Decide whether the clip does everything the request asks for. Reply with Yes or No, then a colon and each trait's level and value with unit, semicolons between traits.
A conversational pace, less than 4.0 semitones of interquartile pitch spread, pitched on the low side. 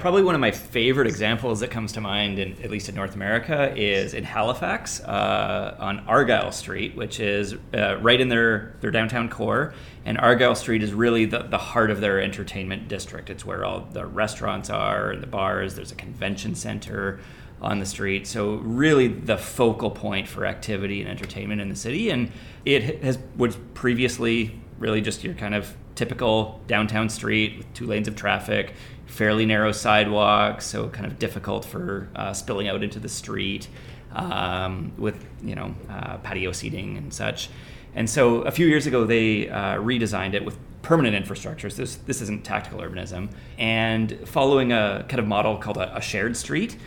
Yes: average, 185 wpm; average, 2.8 semitones; low, 110 Hz